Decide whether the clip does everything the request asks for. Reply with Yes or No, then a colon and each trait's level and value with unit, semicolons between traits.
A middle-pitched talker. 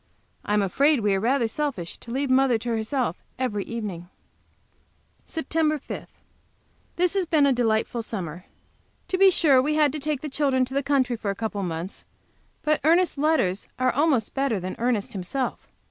No: very high, 255 Hz